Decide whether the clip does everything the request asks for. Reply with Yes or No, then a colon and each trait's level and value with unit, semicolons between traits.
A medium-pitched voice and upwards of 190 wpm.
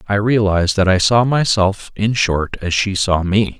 No: low, 100 Hz; average, 200 wpm